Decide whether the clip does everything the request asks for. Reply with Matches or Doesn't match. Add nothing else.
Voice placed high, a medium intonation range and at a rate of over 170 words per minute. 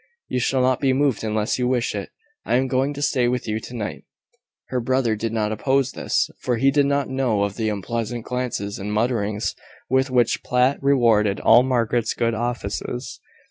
Doesn't match